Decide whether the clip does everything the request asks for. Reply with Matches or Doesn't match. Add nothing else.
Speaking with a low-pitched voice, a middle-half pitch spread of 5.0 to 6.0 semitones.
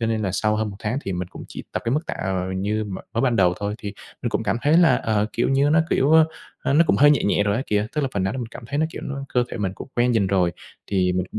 Matches